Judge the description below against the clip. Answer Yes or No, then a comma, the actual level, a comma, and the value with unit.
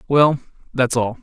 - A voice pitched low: Yes, low, 130 Hz